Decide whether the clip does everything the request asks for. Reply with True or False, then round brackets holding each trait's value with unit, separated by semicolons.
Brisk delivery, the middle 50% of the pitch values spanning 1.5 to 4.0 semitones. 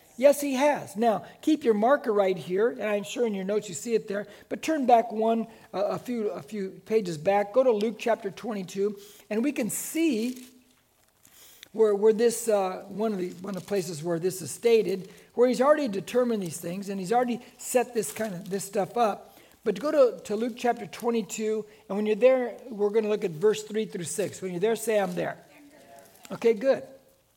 True (215 wpm; 3.1 semitones)